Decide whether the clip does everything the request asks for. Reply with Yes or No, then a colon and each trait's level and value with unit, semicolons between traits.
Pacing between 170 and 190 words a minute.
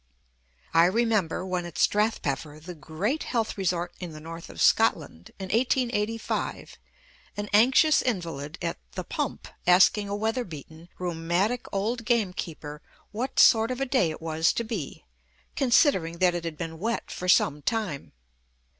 No: average, 150 wpm